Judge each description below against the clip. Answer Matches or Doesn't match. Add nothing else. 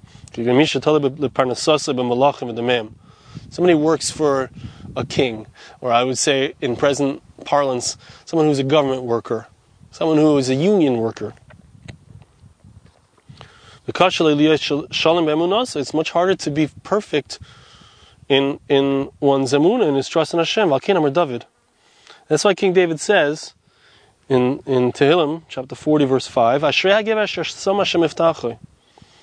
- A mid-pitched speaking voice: Matches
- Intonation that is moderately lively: Matches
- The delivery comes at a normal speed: Doesn't match